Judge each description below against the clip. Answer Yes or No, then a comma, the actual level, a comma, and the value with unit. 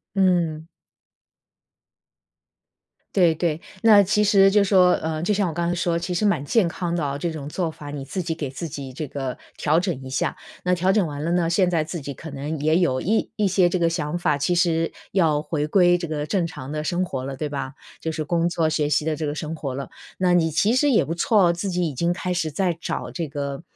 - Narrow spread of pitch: No, average, 3.2 semitones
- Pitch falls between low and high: Yes, medium, 165 Hz